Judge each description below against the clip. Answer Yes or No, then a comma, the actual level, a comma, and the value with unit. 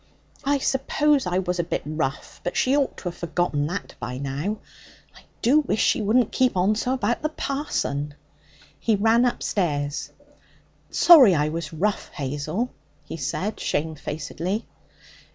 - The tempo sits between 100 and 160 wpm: Yes, average, 150 wpm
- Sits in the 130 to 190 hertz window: Yes, medium, 185 Hz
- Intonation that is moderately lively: No, wide, 8.1 semitones